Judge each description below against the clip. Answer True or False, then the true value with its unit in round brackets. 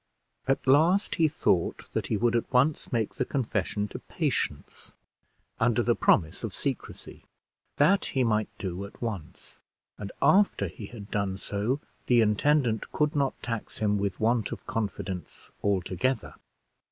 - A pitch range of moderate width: True (4.9 semitones)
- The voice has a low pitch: True (110 Hz)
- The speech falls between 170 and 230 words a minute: False (150 wpm)